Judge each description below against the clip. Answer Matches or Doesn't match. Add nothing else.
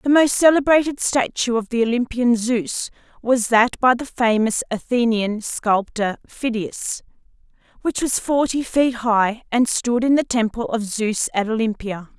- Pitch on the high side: Matches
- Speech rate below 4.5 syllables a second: Matches